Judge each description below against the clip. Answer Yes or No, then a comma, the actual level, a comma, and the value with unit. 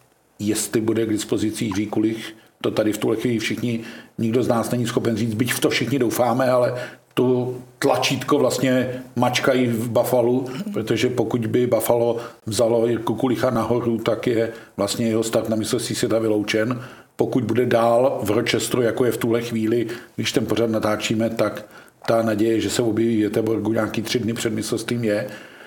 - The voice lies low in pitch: Yes, low, 115 Hz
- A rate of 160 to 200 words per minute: Yes, fast, 170 wpm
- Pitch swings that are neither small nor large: No, narrow, 1.8 semitones